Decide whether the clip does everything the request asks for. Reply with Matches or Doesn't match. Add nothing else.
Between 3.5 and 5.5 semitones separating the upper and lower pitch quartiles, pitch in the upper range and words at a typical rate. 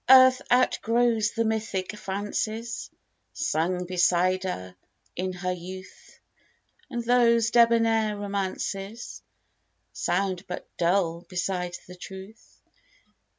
Doesn't match